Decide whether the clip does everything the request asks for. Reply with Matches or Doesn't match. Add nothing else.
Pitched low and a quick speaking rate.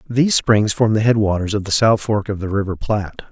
Matches